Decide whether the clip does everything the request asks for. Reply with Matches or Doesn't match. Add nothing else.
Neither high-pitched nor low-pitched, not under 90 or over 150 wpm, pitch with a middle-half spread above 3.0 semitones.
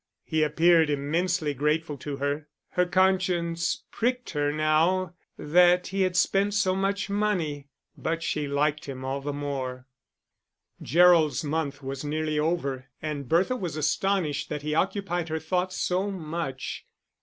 Matches